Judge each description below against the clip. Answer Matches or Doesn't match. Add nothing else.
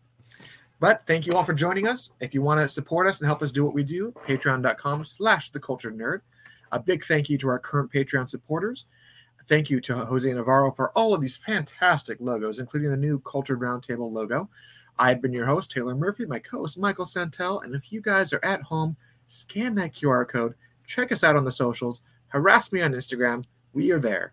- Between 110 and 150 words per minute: Doesn't match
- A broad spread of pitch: Matches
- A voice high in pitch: Doesn't match